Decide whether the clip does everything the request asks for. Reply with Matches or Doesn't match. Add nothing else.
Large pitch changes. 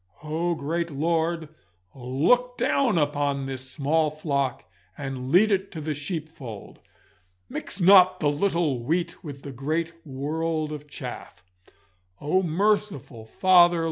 Doesn't match